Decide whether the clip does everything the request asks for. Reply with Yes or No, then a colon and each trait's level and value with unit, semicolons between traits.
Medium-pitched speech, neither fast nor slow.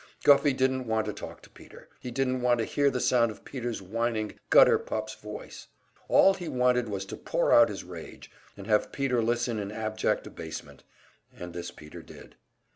No: low, 115 Hz; average, 190 wpm